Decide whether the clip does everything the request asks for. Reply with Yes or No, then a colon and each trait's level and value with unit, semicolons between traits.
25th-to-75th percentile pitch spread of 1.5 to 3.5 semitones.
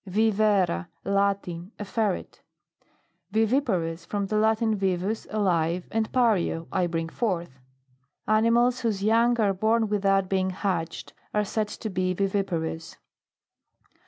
Yes: average, 3.2 semitones